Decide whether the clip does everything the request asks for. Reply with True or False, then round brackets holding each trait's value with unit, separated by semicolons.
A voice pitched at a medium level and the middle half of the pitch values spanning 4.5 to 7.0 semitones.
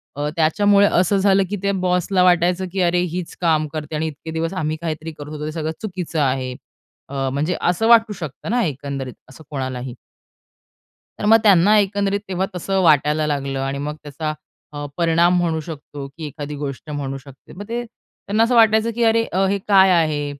True (165 Hz; 4.8 semitones)